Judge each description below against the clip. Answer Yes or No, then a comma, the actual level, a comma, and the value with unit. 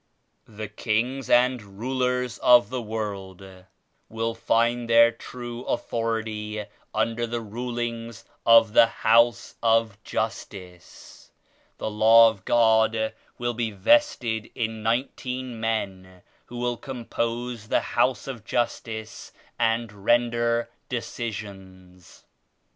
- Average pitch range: No, narrow, 1.8 semitones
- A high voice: No, low, 115 Hz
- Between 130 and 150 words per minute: No, slow, 105 wpm